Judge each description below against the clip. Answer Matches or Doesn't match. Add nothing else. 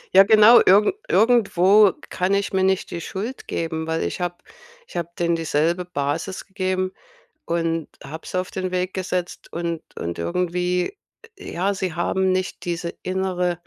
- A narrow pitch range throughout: Matches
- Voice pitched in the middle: Matches